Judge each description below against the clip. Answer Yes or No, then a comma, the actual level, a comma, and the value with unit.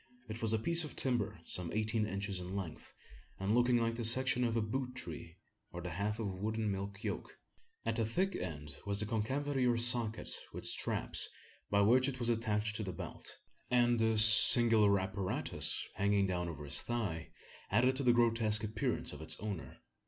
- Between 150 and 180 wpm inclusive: No, average, 190 wpm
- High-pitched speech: No, low, 110 Hz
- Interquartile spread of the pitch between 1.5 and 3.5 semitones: Yes, average, 3.2 semitones